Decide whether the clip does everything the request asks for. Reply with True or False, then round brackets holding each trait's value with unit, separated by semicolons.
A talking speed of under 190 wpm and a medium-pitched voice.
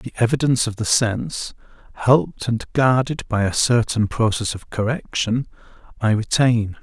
False (140 wpm; 115 Hz)